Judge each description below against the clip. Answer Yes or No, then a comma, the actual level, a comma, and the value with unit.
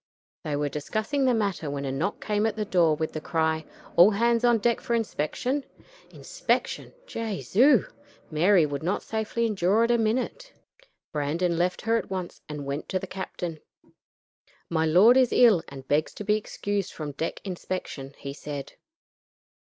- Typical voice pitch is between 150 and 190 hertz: Yes, medium, 185 Hz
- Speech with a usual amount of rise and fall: No, wide, 6.3 semitones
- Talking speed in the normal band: Yes, average, 170 wpm